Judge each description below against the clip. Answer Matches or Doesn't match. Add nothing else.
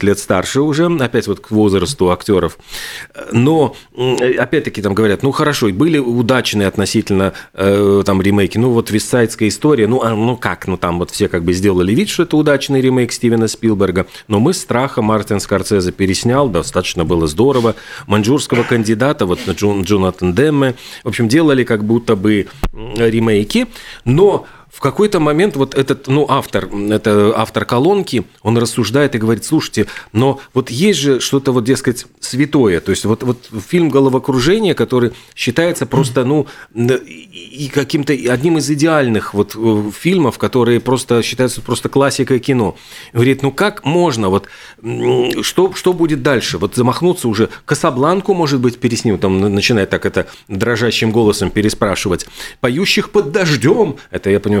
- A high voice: Doesn't match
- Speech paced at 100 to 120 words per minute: Doesn't match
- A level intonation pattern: Doesn't match